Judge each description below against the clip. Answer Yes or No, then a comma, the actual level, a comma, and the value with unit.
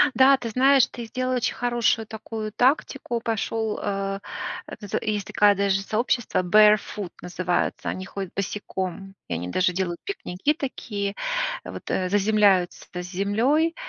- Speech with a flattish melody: No, average, 3.7 semitones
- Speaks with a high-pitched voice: Yes, high, 210 Hz